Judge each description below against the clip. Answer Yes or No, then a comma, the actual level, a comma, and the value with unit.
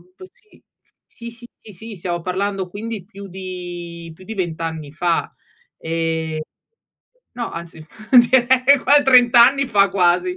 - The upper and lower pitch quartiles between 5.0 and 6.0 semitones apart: Yes, wide, 5.5 semitones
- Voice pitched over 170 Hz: Yes, high, 190 Hz